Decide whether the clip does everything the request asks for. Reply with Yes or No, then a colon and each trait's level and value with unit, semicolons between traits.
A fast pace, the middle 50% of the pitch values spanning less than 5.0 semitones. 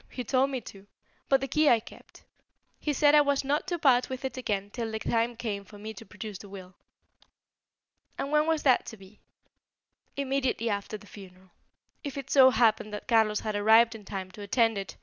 Yes: fast, 210 wpm; average, 4.6 semitones